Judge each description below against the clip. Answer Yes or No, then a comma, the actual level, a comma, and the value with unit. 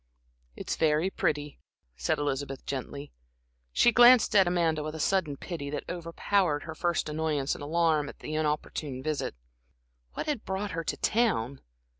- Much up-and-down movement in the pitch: No, average, 3.4 semitones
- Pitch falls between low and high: Yes, medium, 155 Hz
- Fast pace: No, average, 155 wpm